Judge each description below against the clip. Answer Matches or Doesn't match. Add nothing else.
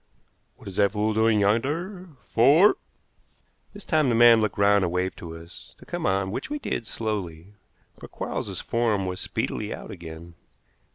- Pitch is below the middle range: Matches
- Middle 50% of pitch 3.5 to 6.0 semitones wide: Matches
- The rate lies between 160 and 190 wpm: Matches